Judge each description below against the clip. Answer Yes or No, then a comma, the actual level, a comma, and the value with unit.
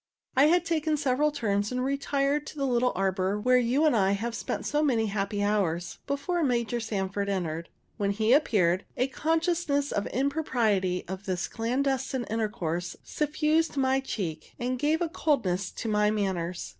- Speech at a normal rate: Yes, average, 170 wpm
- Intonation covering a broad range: Yes, wide, 6.1 semitones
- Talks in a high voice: Yes, high, 235 Hz